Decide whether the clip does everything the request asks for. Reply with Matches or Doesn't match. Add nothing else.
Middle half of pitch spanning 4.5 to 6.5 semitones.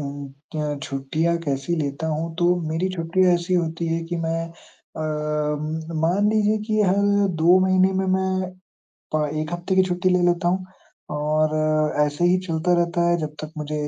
Doesn't match